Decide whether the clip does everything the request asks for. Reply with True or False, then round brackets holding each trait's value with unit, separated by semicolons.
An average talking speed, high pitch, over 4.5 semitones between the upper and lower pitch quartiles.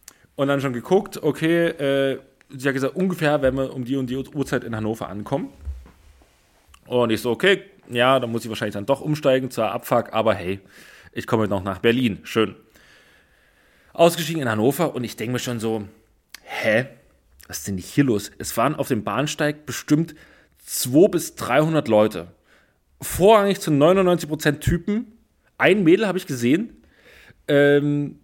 False (165 wpm; 135 Hz; 5.3 semitones)